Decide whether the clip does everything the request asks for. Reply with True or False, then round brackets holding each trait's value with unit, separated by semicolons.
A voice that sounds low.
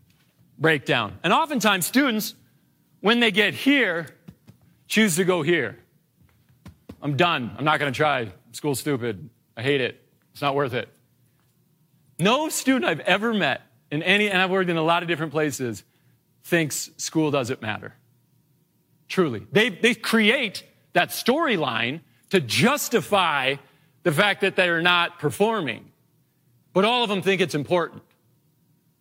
False (165 Hz)